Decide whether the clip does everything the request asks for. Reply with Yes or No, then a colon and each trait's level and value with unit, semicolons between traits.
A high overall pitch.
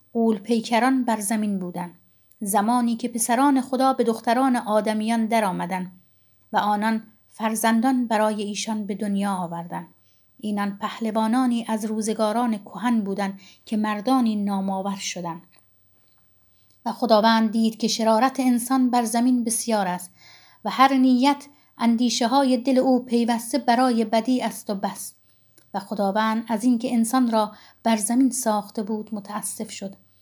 Yes: high, 225 Hz